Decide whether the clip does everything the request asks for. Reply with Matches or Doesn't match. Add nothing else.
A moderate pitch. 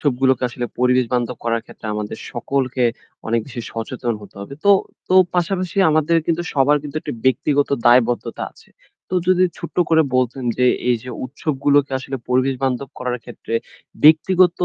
Doesn't match